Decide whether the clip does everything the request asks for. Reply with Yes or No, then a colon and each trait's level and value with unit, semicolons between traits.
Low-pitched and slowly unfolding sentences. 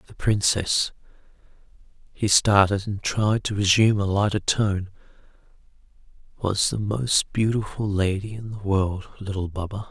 Yes: low, 100 Hz; slow, 115 wpm